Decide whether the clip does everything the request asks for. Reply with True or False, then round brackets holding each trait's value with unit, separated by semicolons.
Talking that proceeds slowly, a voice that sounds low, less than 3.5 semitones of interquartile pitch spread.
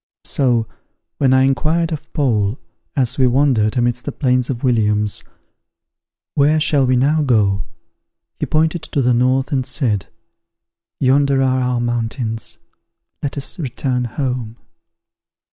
True (130 wpm; 130 Hz; 2.8 semitones)